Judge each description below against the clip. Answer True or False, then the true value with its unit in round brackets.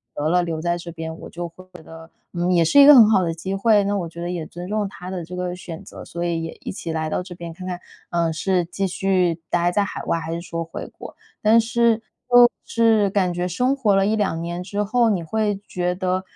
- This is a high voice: False (180 Hz)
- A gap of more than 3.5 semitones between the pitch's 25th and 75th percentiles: False (3.2 semitones)